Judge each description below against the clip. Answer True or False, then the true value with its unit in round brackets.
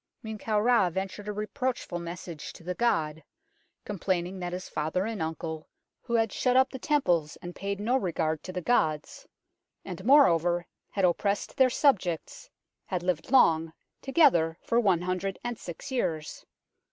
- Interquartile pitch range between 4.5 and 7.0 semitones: True (5.2 semitones)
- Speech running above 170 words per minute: False (160 wpm)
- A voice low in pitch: False (185 Hz)